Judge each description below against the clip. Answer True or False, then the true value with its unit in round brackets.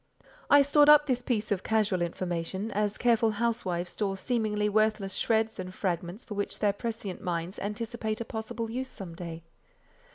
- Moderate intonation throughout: True (3.6 semitones)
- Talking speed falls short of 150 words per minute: False (165 wpm)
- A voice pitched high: True (210 Hz)